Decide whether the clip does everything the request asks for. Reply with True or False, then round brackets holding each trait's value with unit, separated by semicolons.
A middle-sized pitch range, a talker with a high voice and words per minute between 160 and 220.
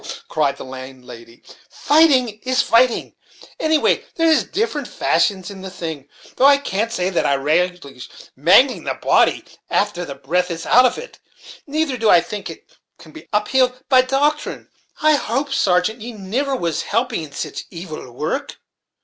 False (8.1 semitones; 210 Hz; 165 wpm)